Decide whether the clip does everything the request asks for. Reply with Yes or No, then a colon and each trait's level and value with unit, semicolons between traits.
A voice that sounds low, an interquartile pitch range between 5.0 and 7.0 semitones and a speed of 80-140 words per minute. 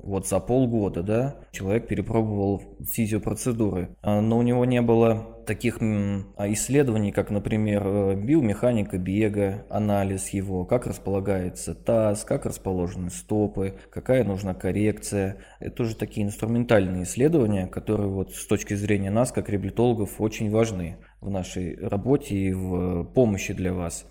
No: low, 100 Hz; average, 2.7 semitones; average, 130 wpm